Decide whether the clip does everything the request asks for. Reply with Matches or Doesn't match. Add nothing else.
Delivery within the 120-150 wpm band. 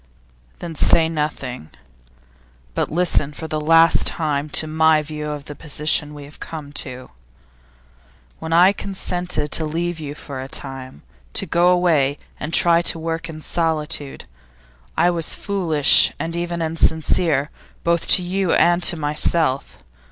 Matches